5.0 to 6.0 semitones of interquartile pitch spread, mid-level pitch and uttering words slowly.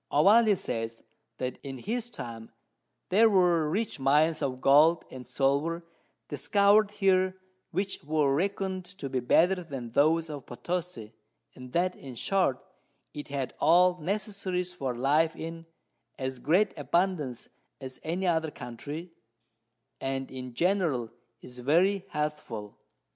Yes: wide, 5.6 semitones; medium, 160 Hz; slow, 130 wpm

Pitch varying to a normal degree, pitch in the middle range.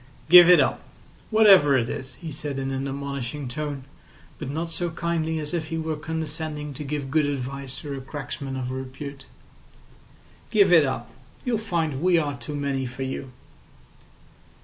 Yes: average, 3.2 semitones; medium, 145 Hz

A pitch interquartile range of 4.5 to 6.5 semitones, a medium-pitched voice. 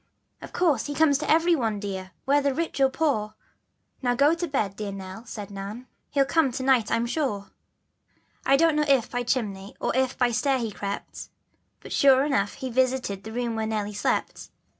No: average, 4.9 semitones; high, 245 Hz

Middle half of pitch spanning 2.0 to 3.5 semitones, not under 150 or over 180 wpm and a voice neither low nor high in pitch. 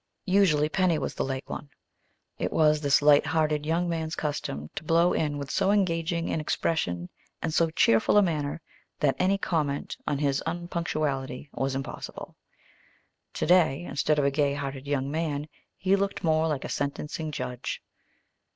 Yes: average, 2.9 semitones; average, 160 wpm; medium, 150 Hz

